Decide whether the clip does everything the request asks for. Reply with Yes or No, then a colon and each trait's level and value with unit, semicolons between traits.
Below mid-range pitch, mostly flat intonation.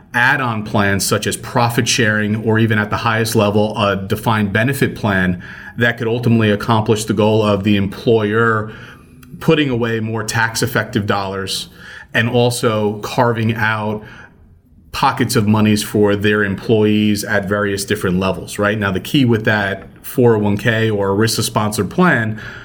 Yes: low, 110 Hz; narrow, 2.1 semitones